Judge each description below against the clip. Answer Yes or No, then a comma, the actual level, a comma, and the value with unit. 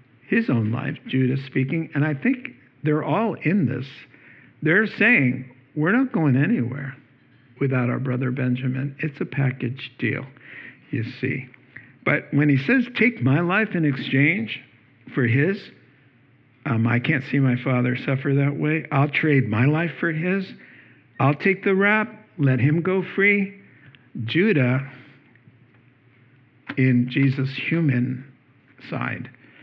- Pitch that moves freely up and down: No, average, 3.5 semitones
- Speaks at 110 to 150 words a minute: Yes, slow, 135 wpm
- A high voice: No, low, 135 Hz